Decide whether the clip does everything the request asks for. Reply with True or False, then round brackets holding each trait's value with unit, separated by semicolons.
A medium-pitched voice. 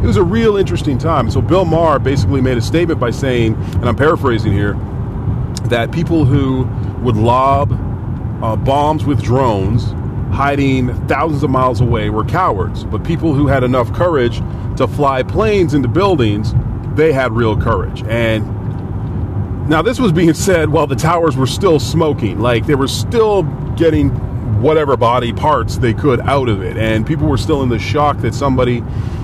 False (120 Hz)